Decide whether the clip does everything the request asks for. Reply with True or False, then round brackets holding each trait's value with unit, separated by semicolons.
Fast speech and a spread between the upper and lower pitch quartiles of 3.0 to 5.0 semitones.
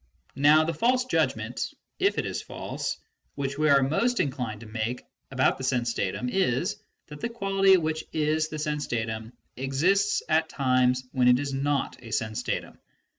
False (175 wpm; 4.4 semitones)